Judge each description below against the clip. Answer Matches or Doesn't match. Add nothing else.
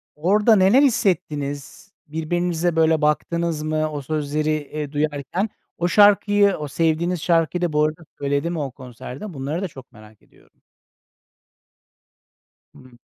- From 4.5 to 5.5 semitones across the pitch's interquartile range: Doesn't match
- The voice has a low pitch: Doesn't match